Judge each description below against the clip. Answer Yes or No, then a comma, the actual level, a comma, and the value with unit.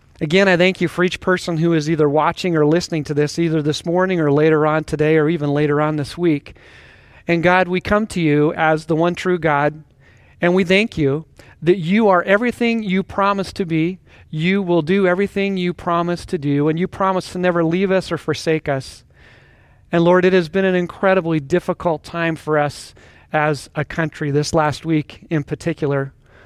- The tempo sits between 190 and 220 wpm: Yes, average, 200 wpm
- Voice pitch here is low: No, medium, 170 Hz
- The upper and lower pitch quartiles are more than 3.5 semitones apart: No, average, 3.2 semitones